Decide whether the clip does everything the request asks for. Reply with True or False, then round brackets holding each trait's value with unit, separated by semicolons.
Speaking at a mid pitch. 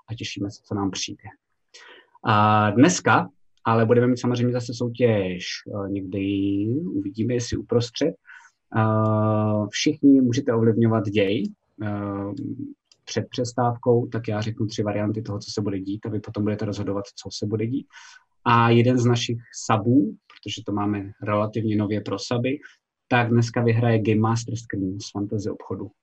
False (110 Hz)